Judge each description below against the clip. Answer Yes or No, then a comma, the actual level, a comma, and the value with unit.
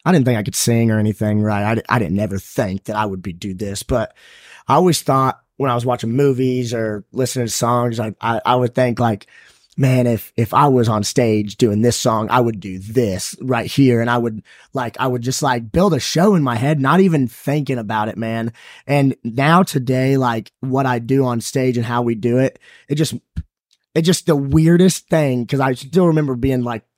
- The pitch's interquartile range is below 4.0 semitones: Yes, average, 3.3 semitones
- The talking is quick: Yes, fast, 225 wpm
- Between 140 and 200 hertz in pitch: No, low, 125 Hz